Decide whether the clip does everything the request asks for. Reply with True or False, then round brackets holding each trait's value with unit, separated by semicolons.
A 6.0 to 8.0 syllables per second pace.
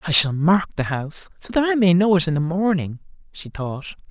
False (5.4 syllables/s)